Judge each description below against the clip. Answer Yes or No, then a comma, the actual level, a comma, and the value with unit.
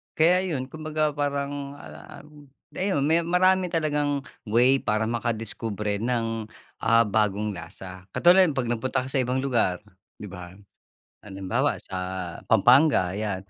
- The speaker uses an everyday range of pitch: No, wide, 5.9 semitones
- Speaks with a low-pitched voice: Yes, low, 130 Hz